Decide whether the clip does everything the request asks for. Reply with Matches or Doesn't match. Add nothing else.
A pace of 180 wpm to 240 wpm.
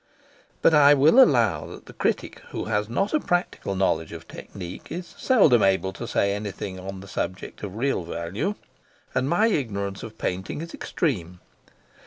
Doesn't match